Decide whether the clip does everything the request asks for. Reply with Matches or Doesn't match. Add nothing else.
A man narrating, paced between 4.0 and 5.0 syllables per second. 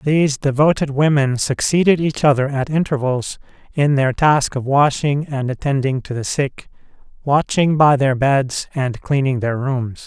Matches